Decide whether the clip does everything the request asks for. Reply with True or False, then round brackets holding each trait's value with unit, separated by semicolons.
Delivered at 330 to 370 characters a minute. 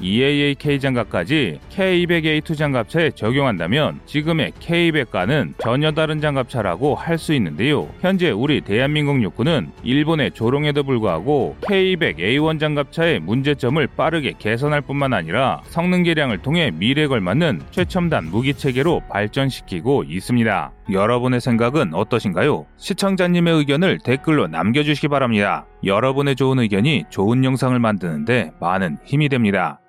True (340 characters per minute)